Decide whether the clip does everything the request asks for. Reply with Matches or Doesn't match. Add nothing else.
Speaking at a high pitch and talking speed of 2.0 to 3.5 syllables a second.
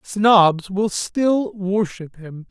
Matches